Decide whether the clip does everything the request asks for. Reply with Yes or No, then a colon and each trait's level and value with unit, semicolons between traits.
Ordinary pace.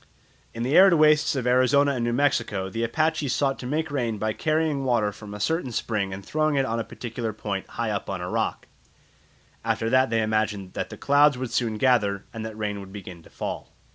No: fast, 220 wpm